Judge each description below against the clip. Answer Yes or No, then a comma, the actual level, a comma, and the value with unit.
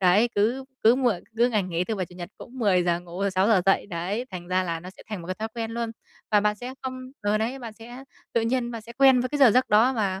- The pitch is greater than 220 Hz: No, high, 215 Hz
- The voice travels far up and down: No, average, 4.5 semitones